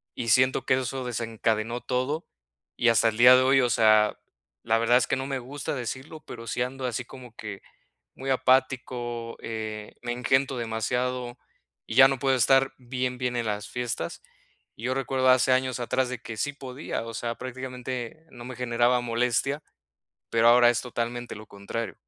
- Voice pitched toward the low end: Yes, low, 125 Hz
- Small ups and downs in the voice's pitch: Yes, narrow, 1.9 semitones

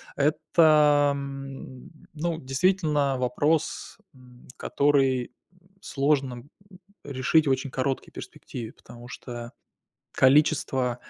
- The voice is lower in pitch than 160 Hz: Yes, low, 135 Hz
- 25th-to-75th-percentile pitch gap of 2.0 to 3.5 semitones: Yes, average, 2.7 semitones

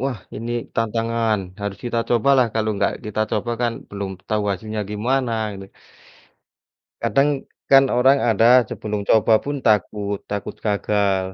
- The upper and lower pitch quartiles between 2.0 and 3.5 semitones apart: Yes, average, 2.8 semitones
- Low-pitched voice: Yes, low, 110 Hz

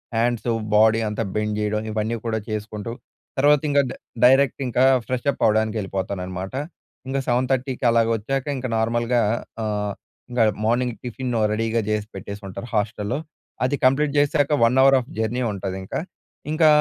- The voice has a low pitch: Yes, low, 115 Hz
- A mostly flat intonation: No, average, 3.3 semitones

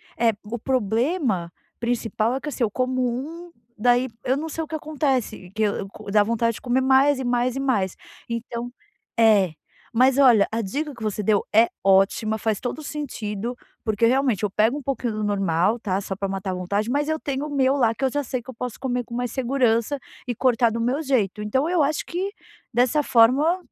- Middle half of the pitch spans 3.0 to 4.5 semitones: Yes, average, 4.0 semitones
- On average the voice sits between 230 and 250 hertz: Yes, high, 240 Hz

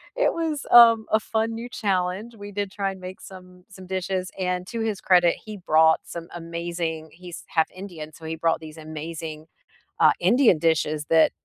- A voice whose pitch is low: No, medium, 180 Hz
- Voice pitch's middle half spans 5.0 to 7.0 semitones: No, average, 3.9 semitones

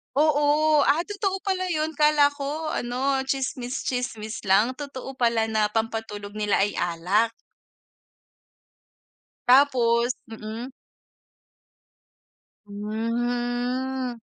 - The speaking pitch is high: Yes, high, 245 Hz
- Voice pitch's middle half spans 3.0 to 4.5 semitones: Yes, average, 4.2 semitones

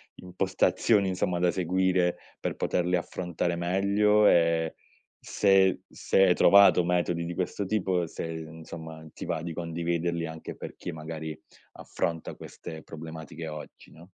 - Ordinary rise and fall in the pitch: No, narrow, 2.2 semitones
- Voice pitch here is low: Yes, very low, 85 Hz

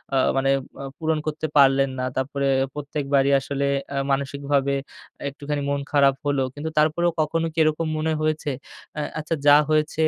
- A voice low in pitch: No, medium, 145 Hz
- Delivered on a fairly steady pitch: Yes, narrow, 1.9 semitones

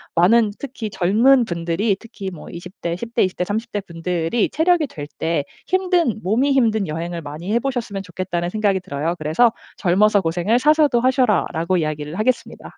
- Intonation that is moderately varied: No, wide, 5.7 semitones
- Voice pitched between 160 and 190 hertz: No, high, 200 Hz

